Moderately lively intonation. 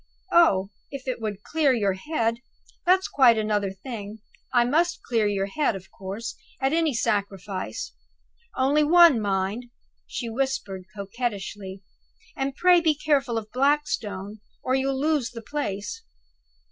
No: wide, 6.0 semitones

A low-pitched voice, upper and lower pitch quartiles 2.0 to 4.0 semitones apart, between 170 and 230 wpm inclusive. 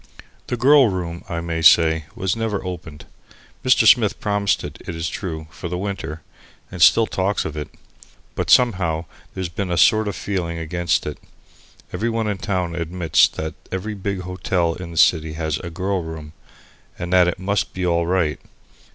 Yes: very low, 90 Hz; average, 3.3 semitones; average, 180 wpm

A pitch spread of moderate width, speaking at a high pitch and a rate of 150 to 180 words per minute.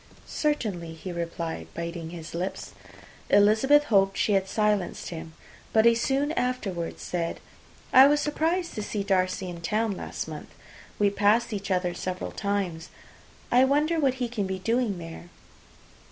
No: wide, 5.8 semitones; high, 200 Hz; average, 155 wpm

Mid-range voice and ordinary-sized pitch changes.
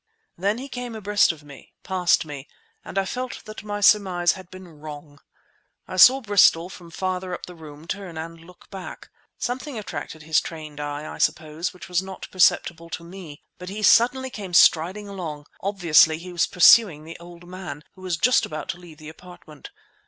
Yes: medium, 180 Hz; average, 3.6 semitones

